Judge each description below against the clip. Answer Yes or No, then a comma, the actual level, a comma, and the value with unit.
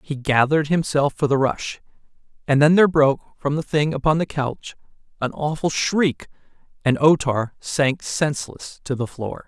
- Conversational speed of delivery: Yes, average, 165 wpm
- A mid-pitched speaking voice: Yes, medium, 145 Hz